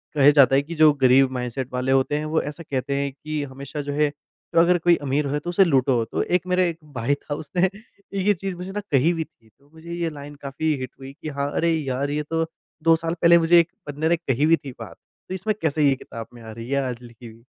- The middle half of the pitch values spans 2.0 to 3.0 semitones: No, average, 3.8 semitones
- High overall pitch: No, medium, 145 Hz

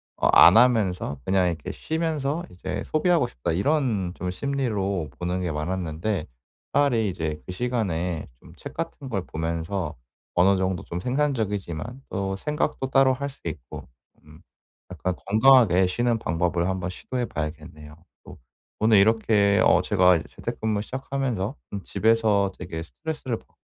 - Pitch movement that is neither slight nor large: No, wide, 6.0 semitones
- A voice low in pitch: Yes, low, 100 Hz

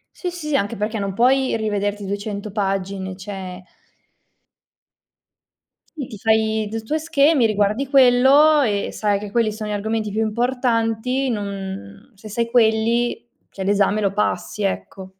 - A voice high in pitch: Yes, high, 215 Hz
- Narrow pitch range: No, average, 3.2 semitones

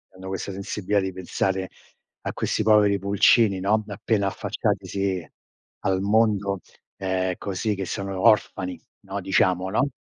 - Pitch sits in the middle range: No, low, 100 Hz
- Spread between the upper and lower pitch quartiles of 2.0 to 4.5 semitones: No, narrow, 1.5 semitones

